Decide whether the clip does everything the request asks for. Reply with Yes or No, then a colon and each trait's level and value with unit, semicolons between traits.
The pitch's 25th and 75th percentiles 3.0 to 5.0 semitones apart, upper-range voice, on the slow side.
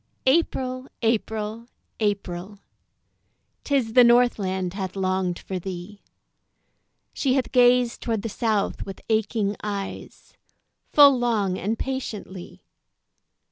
Yes: average, 4.0 semitones; high, 215 Hz; slow, 100 wpm